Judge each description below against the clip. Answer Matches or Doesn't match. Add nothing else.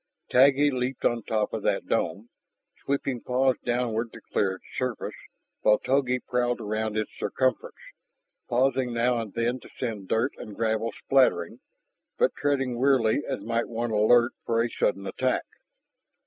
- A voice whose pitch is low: Matches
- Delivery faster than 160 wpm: Doesn't match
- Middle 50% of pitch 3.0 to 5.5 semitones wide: Doesn't match